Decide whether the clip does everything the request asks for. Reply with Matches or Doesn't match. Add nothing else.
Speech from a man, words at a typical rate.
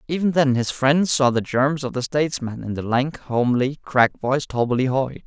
Matches